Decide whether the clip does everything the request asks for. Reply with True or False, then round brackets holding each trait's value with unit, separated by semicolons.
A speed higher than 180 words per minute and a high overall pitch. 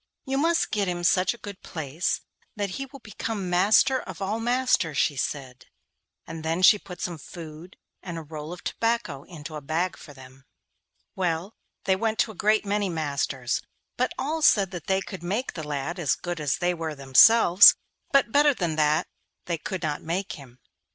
False (190 wpm; 175 Hz)